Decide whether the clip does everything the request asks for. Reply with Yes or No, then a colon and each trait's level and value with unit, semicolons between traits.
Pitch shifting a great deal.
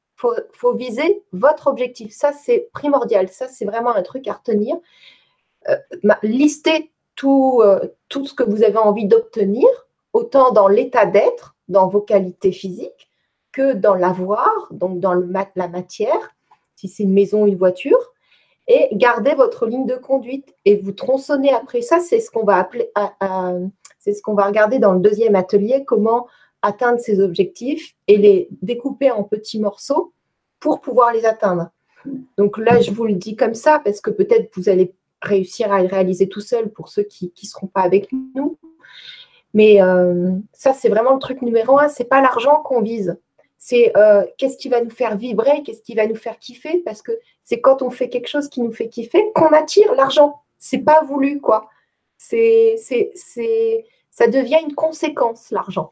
Yes: wide, 6.7 semitones